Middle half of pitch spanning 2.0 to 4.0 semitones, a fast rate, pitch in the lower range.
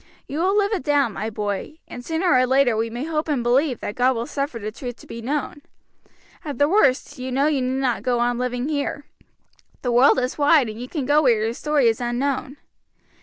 No: average, 3.3 semitones; fast, 225 wpm; very high, 255 Hz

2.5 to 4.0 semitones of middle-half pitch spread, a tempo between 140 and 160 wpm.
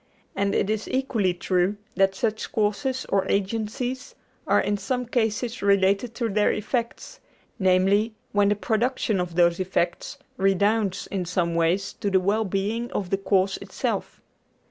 Yes: average, 2.9 semitones; average, 150 wpm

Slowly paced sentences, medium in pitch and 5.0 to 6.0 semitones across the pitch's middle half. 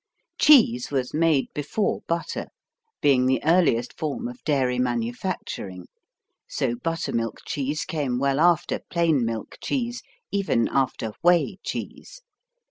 Yes: slow, 120 wpm; medium, 145 Hz; wide, 5.5 semitones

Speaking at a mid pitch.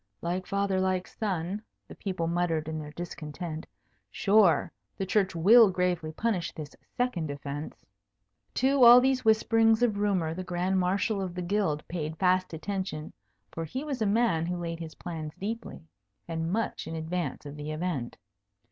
Yes: medium, 180 Hz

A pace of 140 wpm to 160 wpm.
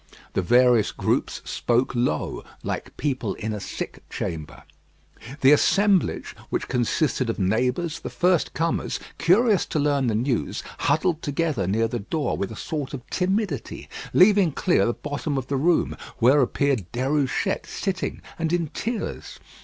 Yes: average, 150 wpm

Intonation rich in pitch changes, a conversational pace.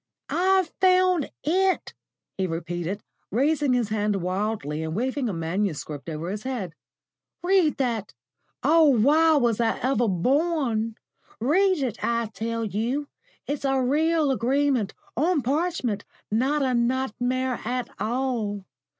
No: wide, 5.7 semitones; slow, 125 wpm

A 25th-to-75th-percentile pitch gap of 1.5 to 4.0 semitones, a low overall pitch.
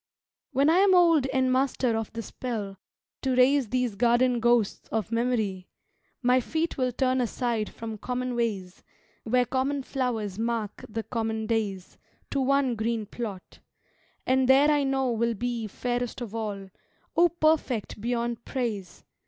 No: average, 2.8 semitones; high, 240 Hz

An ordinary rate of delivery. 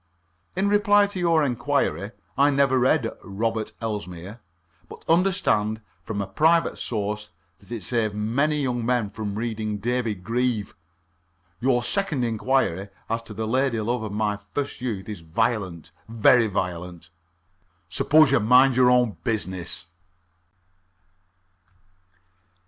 No: slow, 125 wpm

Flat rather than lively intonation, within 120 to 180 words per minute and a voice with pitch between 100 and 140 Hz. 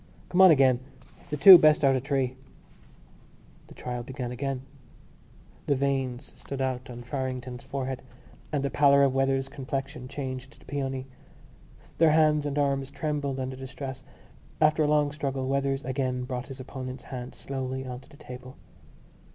Yes: narrow, 1.6 semitones; average, 160 wpm; low, 135 Hz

